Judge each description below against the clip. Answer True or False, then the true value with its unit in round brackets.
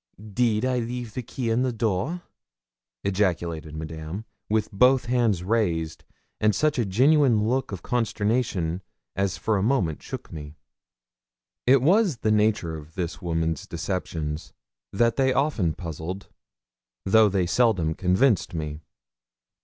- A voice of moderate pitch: False (105 Hz)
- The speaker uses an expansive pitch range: True (6.4 semitones)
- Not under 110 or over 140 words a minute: True (135 wpm)